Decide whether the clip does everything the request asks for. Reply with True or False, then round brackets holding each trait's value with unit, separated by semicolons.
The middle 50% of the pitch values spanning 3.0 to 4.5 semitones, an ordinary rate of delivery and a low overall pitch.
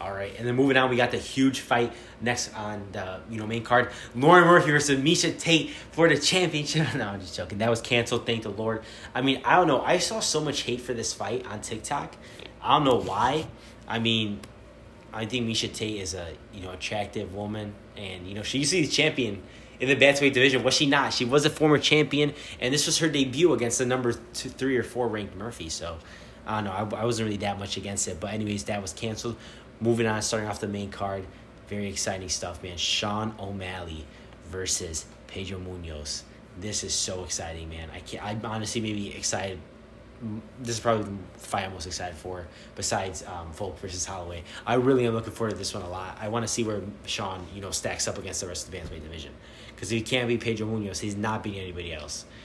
False (4.0 semitones; 230 wpm; 110 Hz)